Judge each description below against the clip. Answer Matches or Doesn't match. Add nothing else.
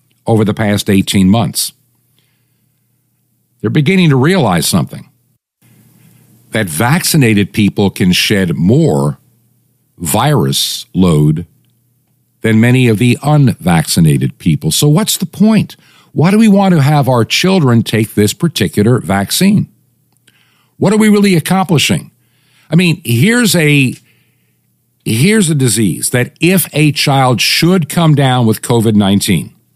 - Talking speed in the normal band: Doesn't match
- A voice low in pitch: Matches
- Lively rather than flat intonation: Matches